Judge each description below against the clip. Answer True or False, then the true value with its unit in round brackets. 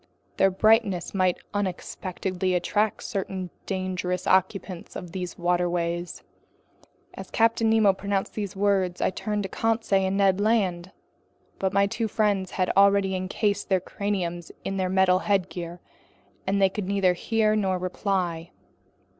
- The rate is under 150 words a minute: True (140 wpm)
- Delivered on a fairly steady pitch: True (1.8 semitones)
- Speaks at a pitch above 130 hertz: True (190 Hz)